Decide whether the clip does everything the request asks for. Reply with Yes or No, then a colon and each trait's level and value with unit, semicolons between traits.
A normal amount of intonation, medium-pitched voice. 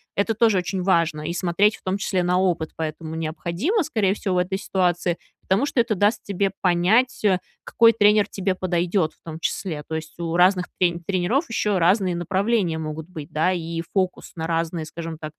Yes: average, 3.2 semitones; medium, 180 Hz